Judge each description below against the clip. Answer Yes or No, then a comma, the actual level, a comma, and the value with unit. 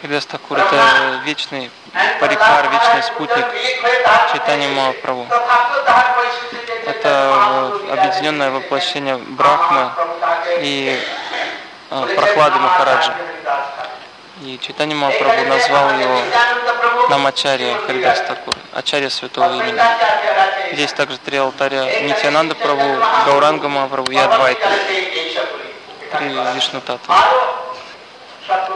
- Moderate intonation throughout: No, wide, 8.3 semitones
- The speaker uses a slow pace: Yes, slow, 80 wpm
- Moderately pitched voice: Yes, medium, 165 Hz